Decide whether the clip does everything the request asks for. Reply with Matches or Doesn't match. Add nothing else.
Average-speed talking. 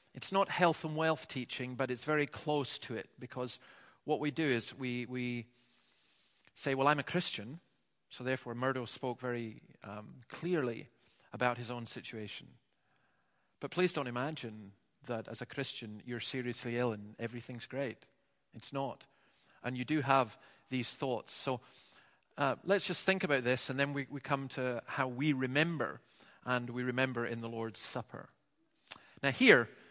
Matches